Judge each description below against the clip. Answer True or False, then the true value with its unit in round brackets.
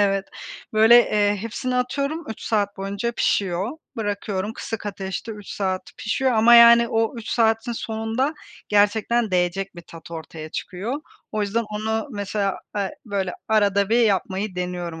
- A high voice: True (210 Hz)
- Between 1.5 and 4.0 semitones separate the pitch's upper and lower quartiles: True (2.8 semitones)